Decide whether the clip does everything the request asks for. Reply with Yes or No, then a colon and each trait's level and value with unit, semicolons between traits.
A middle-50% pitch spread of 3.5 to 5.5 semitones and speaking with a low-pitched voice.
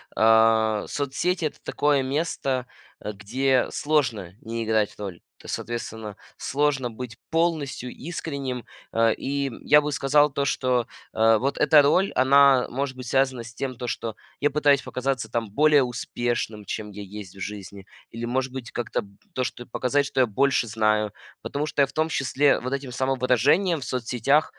Yes: average, 3.9 semitones; low, 130 Hz